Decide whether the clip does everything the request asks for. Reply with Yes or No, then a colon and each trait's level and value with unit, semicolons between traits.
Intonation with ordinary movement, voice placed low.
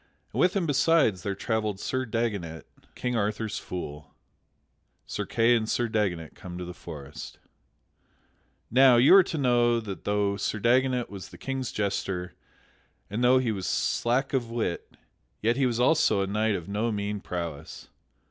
Yes: average, 4.1 semitones; low, 110 Hz